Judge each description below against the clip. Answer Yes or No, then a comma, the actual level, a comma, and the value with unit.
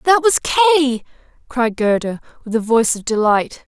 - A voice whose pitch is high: Yes, very high, 255 Hz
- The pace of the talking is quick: No, average, 160 wpm